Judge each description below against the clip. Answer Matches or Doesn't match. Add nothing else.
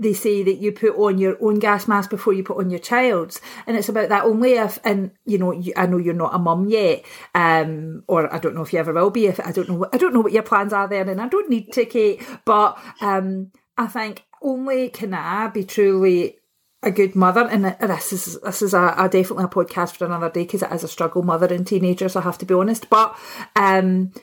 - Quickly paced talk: Matches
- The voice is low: Doesn't match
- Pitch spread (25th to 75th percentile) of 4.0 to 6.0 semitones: Doesn't match